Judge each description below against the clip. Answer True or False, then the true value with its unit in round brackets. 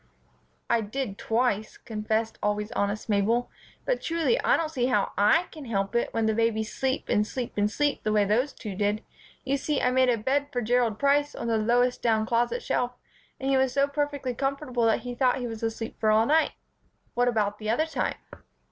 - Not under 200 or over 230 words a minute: True (205 wpm)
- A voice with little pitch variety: False (3.6 semitones)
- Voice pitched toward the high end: True (240 Hz)